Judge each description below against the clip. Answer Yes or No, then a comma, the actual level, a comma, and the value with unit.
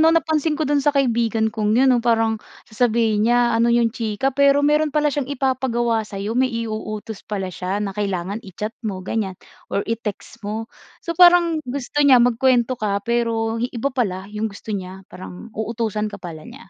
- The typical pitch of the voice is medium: No, high, 230 Hz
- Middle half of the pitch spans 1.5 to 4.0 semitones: Yes, average, 3.7 semitones